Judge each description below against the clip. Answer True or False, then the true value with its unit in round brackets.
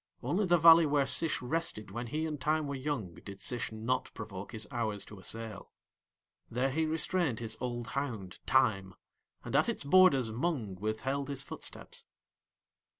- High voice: False (125 Hz)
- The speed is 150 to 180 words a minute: True (160 wpm)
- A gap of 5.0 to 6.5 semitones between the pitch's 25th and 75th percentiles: True (5.6 semitones)